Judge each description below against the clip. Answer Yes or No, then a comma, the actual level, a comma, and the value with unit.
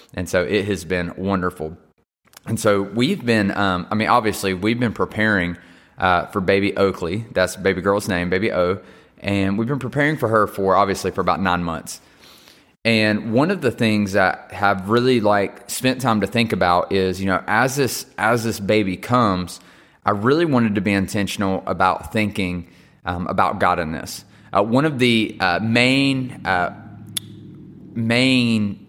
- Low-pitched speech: Yes, low, 100 Hz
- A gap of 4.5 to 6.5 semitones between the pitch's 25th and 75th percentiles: No, average, 3.8 semitones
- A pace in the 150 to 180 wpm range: Yes, average, 175 wpm